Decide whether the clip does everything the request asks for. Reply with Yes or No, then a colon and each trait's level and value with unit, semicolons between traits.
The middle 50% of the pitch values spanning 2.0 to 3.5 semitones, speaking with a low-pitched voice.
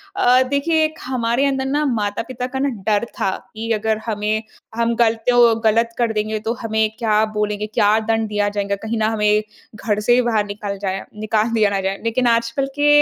No: narrow, 2.5 semitones; high, 225 Hz